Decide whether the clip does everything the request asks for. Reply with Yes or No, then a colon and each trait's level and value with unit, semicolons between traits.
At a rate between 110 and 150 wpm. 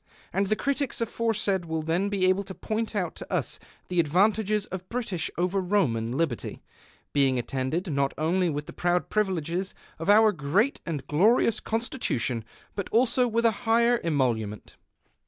No: average, 160 wpm